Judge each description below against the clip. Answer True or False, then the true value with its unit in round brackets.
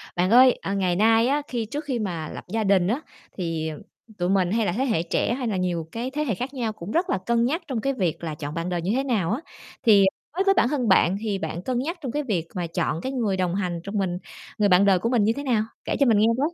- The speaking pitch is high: True (210 Hz)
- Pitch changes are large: True (5.9 semitones)